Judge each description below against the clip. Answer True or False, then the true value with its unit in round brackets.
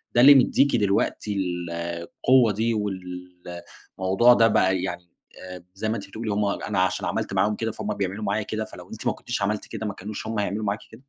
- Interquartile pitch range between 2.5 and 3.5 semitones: True (2.9 semitones)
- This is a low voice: True (105 Hz)